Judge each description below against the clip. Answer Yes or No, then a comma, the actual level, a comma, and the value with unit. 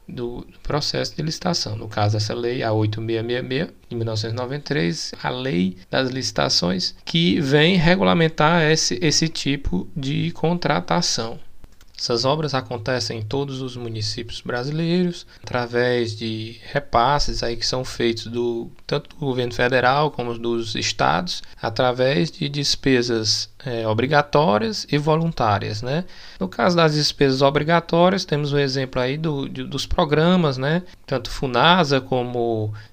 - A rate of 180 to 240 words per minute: No, average, 130 wpm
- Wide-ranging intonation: No, average, 4.7 semitones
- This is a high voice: No, low, 130 Hz